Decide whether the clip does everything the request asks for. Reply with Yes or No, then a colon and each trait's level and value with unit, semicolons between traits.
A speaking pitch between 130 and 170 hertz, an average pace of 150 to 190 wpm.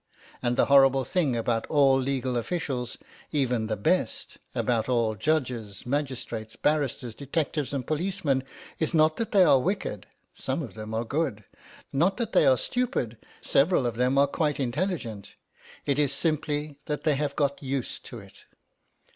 Yes: low, 135 Hz; average, 160 wpm